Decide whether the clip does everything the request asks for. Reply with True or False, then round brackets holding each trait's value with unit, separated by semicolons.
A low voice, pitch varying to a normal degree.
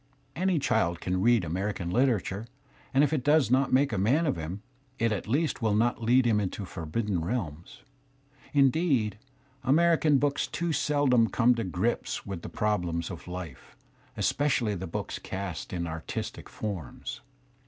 False (110 Hz; 6.7 semitones)